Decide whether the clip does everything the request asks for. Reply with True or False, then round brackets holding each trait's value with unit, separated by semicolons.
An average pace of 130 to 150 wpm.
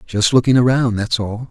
False (200 wpm)